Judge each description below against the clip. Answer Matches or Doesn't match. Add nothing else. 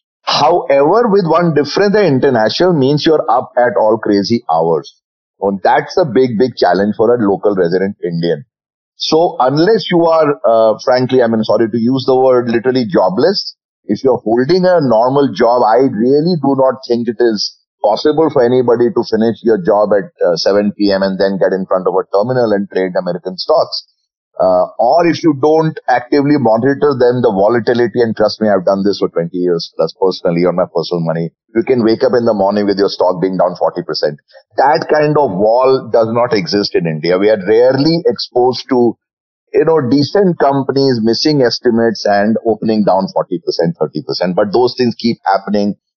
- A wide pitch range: Matches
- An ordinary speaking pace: Matches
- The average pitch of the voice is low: Matches